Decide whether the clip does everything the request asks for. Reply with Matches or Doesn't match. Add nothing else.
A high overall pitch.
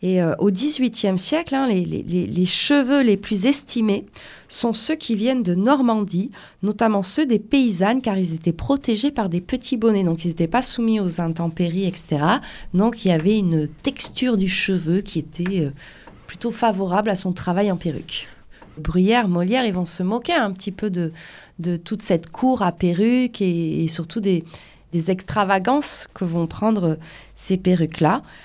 Matches